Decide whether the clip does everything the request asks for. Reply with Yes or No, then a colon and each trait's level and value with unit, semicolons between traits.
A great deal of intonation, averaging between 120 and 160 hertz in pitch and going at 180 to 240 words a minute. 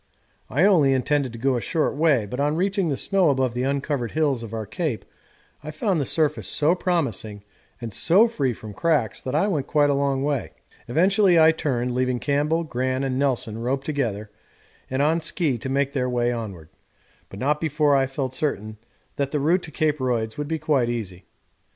No: average, 4.1 semitones; medium, 140 Hz; average, 200 wpm